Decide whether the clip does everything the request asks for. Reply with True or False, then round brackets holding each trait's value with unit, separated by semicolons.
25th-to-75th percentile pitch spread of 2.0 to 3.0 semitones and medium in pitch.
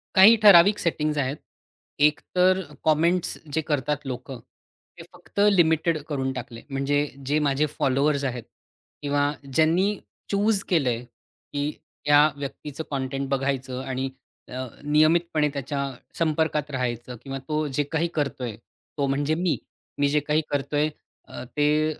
True (2.6 semitones; 145 Hz)